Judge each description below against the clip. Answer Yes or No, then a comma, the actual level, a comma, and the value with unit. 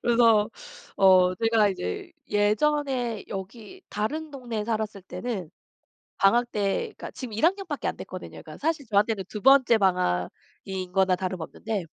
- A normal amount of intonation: Yes, average, 4.4 semitones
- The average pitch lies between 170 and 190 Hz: No, high, 215 Hz